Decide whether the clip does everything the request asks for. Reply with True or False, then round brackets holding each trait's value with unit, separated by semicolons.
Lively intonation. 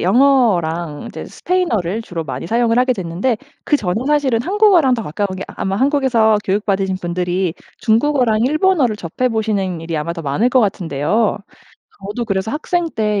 True (6.0 semitones)